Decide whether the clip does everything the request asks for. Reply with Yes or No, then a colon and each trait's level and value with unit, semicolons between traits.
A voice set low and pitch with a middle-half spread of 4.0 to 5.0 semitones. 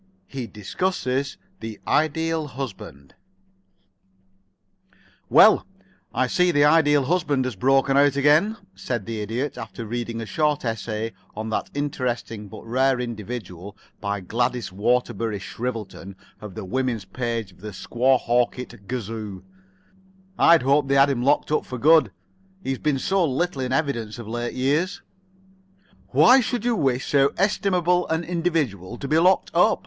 Yes: low, 130 Hz; average, 4.7 semitones